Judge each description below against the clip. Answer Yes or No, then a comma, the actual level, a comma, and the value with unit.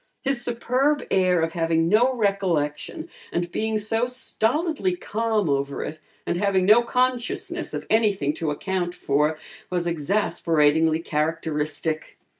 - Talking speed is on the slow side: Yes, slow, 125 wpm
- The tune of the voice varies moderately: No, wide, 6.2 semitones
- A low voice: No, medium, 185 Hz